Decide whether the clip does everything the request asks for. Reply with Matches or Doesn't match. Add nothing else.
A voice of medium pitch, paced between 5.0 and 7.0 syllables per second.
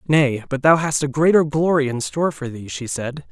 Matches